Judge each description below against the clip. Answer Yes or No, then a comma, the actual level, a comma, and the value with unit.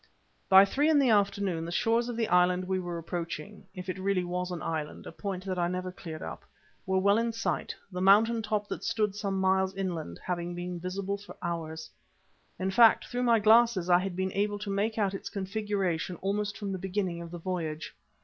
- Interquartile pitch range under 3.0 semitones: Yes, narrow, 2.6 semitones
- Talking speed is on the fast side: Yes, fast, 210 wpm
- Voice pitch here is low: No, high, 190 Hz